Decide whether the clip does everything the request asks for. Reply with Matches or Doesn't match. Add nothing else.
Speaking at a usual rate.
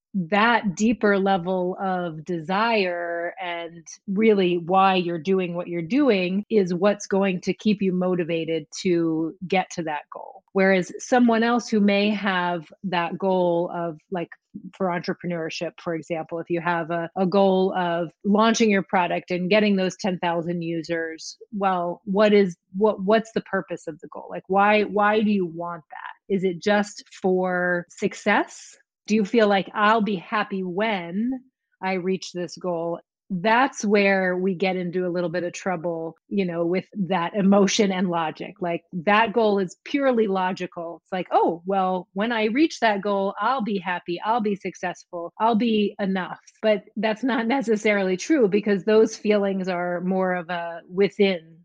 Matches